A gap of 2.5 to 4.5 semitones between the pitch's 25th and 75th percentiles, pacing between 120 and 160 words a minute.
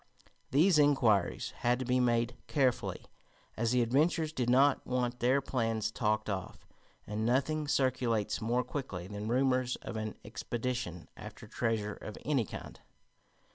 Yes: average, 3.1 semitones; average, 140 wpm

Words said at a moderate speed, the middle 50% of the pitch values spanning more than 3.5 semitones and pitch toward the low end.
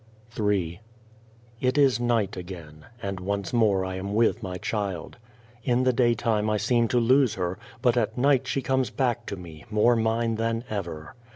Yes: average, 175 wpm; average, 4.0 semitones; low, 110 Hz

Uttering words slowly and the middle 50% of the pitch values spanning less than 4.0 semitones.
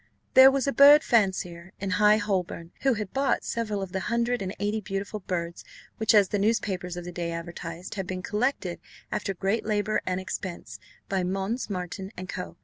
No: average, 190 wpm; average, 3.0 semitones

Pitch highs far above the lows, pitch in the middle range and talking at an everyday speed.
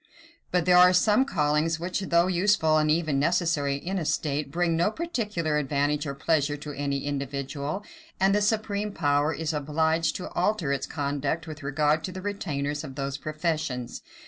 No: average, 3.7 semitones; medium, 155 Hz; average, 175 wpm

